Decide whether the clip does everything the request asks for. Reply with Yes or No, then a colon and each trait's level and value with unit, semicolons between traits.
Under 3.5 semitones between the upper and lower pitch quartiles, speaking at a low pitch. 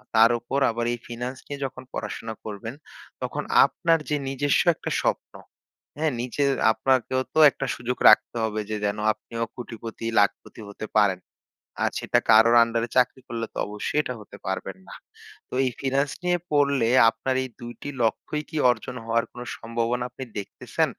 Yes: average, 2.8 semitones; low, 120 Hz